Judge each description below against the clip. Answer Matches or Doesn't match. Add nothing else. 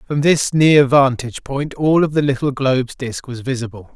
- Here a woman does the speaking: Doesn't match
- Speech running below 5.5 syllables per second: Matches